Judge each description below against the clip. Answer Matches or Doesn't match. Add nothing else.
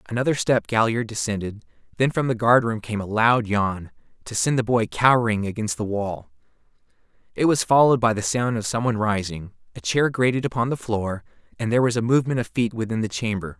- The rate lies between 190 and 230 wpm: Matches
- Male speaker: Matches